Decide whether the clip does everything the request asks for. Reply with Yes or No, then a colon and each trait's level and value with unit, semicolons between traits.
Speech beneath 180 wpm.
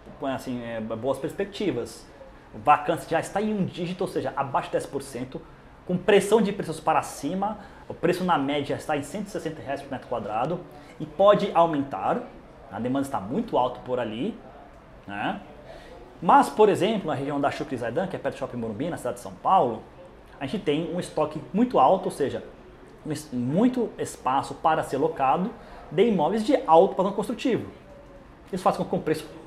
No: fast, 185 wpm